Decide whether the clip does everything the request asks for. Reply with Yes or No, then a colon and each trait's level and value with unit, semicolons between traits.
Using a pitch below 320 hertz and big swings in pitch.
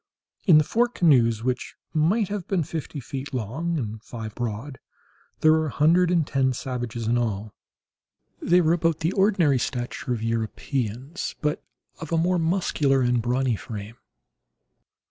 Yes: low, 135 Hz; wide, 5.7 semitones